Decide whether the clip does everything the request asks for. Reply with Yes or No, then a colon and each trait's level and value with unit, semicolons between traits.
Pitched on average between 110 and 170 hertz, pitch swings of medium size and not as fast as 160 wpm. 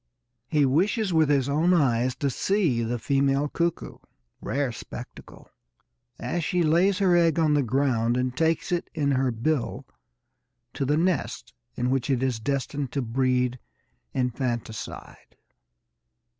Yes: medium, 140 Hz; average, 4.2 semitones; average, 140 wpm